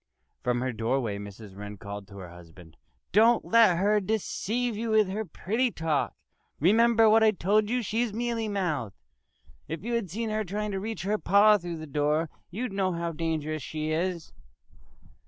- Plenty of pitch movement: Yes, wide, 6.4 semitones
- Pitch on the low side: No, medium, 185 Hz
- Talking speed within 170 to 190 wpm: Yes, average, 175 wpm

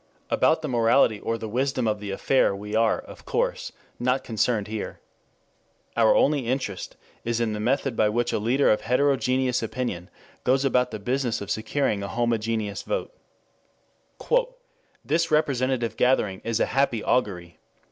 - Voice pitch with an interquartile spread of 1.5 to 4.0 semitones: Yes, average, 3.5 semitones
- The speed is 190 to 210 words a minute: No, average, 155 wpm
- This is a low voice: Yes, low, 115 Hz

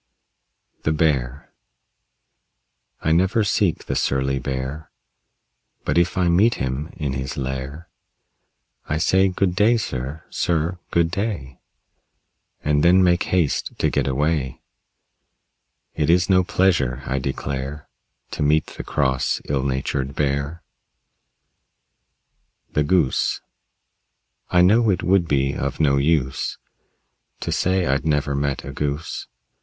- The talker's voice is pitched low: Yes, very low, 75 Hz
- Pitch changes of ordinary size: Yes, average, 4.5 semitones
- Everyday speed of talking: No, slow, 125 wpm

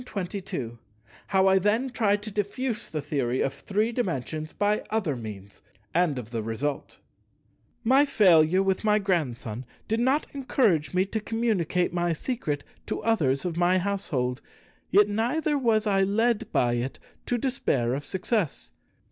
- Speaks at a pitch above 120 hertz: Yes, high, 190 Hz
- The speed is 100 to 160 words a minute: Yes, average, 155 wpm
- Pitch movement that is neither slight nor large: No, wide, 7.3 semitones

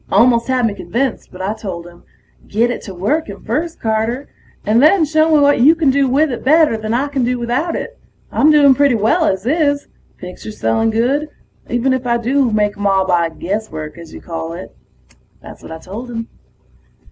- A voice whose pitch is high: Yes, high, 235 Hz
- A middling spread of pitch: No, wide, 5.8 semitones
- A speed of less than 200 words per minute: No, fast, 205 wpm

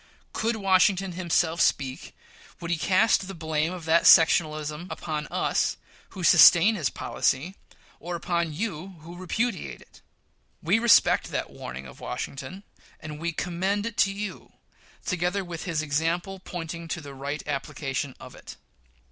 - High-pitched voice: No, medium, 170 Hz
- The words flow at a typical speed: Yes, average, 150 wpm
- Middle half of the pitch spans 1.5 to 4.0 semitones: Yes, average, 3.4 semitones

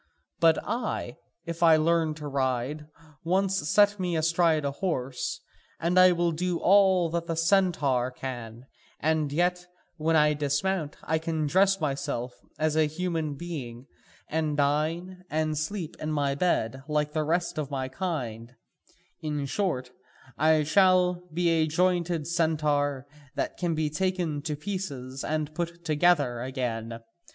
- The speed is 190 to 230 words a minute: No, average, 145 wpm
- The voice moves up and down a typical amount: Yes, average, 3.4 semitones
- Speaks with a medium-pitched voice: Yes, medium, 155 Hz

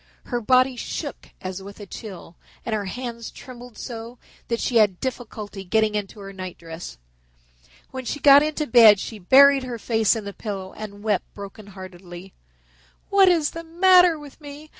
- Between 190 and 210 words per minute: No, average, 165 wpm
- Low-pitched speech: No, high, 225 Hz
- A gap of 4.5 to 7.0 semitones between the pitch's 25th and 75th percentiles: Yes, average, 4.9 semitones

